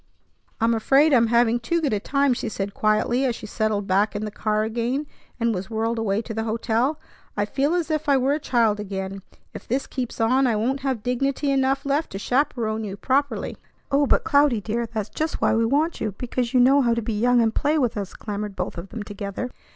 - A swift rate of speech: Yes, fast, 230 wpm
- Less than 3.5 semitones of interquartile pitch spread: No, average, 4.1 semitones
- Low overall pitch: No, high, 235 Hz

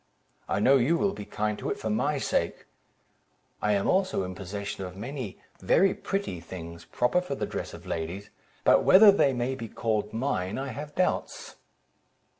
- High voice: No, low, 115 Hz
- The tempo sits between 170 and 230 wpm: Yes, average, 180 wpm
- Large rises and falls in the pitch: Yes, wide, 6.5 semitones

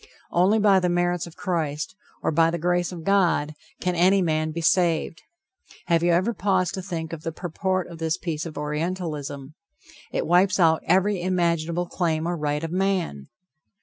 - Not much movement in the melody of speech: Yes, narrow, 2.3 semitones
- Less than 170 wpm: No, average, 180 wpm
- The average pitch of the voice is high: No, medium, 170 Hz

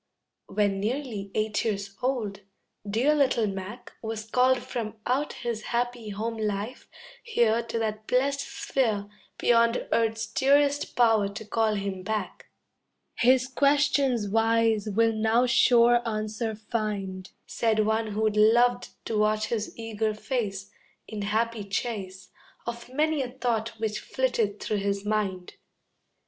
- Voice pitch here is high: Yes, high, 225 Hz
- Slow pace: Yes, slow, 130 wpm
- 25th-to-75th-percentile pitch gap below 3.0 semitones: Yes, narrow, 2.5 semitones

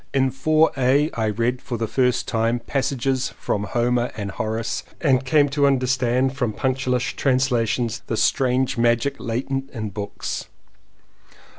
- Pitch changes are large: No, narrow, 2.4 semitones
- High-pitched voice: No, low, 125 Hz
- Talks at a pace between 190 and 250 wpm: No, average, 145 wpm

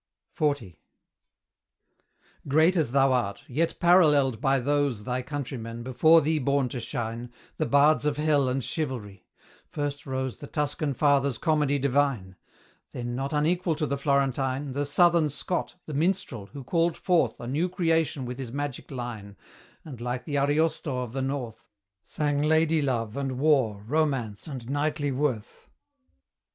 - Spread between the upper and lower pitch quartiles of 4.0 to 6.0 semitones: No, average, 3.3 semitones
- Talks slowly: No, average, 150 wpm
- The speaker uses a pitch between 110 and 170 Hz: Yes, medium, 140 Hz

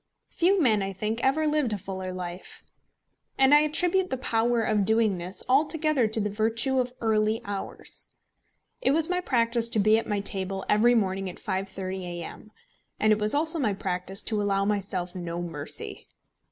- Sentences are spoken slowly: No, average, 180 wpm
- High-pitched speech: Yes, high, 215 Hz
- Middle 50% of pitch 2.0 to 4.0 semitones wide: No, average, 4.9 semitones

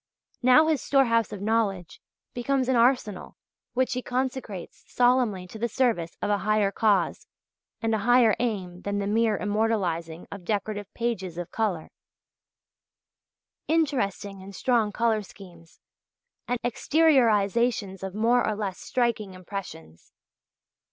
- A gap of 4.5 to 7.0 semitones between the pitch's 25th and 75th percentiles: No, average, 3.9 semitones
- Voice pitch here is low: No, high, 215 Hz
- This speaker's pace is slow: Yes, slow, 130 wpm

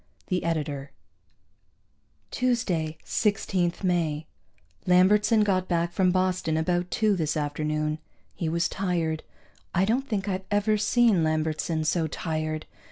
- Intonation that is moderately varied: Yes, average, 3.7 semitones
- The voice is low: No, medium, 175 Hz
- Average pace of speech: No, slow, 120 wpm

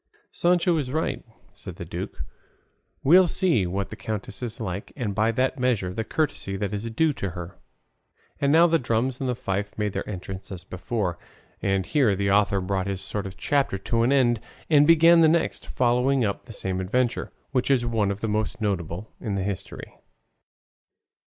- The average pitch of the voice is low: Yes, low, 110 Hz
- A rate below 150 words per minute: No, average, 185 wpm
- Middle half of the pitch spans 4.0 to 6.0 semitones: Yes, average, 5.2 semitones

